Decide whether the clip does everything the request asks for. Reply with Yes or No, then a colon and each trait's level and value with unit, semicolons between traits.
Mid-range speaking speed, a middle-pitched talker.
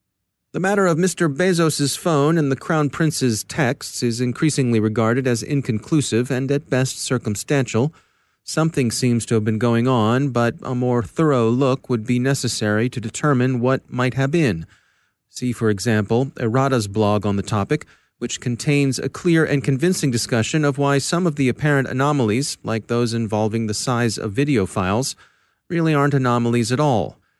No: average, 165 wpm; low, 130 Hz